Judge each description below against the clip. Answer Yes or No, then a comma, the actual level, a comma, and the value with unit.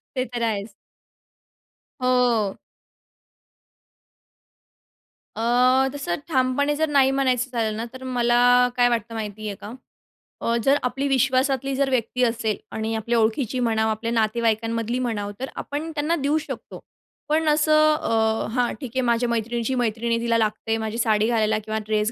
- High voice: Yes, high, 240 Hz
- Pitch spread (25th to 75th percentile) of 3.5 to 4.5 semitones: No, average, 2.9 semitones